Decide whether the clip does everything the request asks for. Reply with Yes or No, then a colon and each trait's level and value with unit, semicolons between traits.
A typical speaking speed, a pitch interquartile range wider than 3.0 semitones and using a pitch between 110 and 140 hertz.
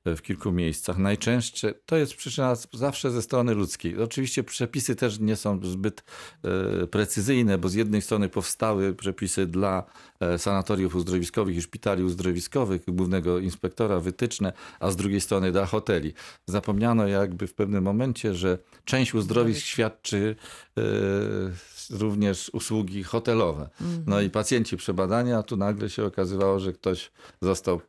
No: average, 140 wpm; average, 3.4 semitones; low, 100 Hz